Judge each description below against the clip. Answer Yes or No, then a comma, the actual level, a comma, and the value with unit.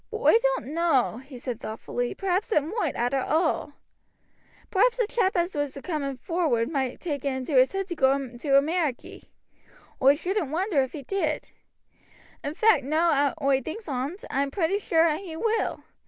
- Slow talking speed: No, average, 185 wpm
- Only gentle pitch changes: No, average, 5.1 semitones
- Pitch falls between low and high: No, very high, 305 Hz